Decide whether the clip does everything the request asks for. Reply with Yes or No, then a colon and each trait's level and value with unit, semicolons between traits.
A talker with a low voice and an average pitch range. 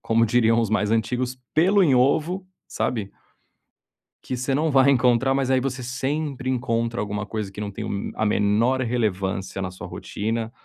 Yes: low, 120 Hz; average, 3.9 semitones